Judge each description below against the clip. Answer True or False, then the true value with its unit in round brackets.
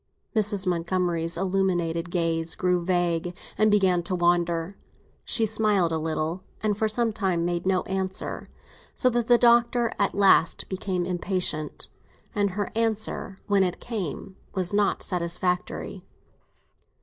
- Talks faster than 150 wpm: False (135 wpm)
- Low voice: False (185 Hz)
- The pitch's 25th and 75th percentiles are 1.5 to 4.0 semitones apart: True (3.0 semitones)